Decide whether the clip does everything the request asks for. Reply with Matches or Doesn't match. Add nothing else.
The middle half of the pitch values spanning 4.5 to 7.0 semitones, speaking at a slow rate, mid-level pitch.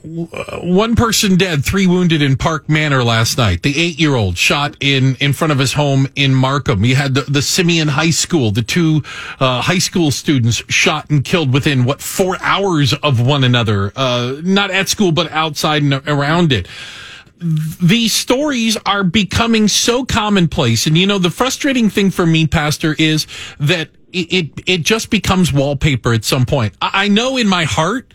Doesn't match